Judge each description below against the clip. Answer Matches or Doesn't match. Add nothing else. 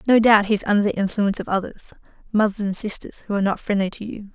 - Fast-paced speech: Matches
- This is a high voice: Matches